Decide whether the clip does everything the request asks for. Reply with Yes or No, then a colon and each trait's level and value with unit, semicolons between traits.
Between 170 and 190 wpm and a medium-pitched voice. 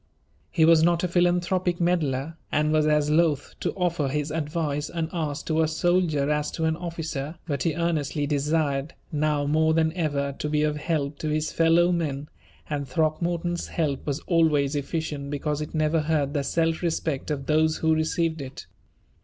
Yes: average, 175 wpm; medium, 155 Hz